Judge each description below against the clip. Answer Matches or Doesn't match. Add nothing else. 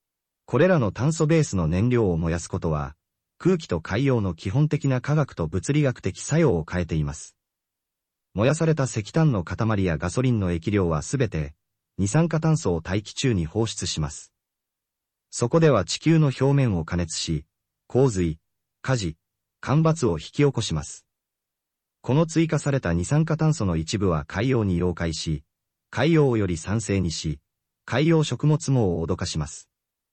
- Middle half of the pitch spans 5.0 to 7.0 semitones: Doesn't match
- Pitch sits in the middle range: Doesn't match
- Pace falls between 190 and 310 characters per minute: Matches